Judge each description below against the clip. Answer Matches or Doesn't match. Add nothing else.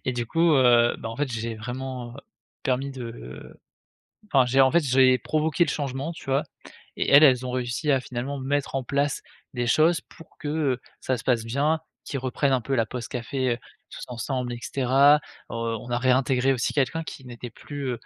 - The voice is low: Matches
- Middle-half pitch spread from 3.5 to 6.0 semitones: Doesn't match